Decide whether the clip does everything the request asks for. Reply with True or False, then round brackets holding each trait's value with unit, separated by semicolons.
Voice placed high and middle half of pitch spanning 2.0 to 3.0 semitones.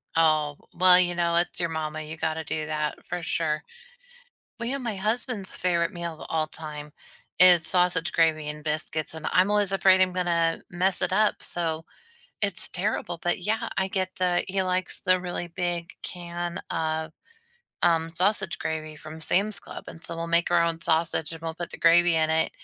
False (170 Hz; 2.4 semitones)